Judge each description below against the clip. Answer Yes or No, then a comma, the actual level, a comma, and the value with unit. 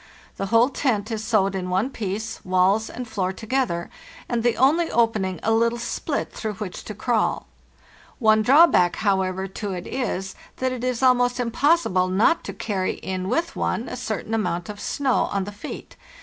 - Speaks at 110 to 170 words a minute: No, average, 180 wpm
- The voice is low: No, high, 220 Hz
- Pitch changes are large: No, average, 4.3 semitones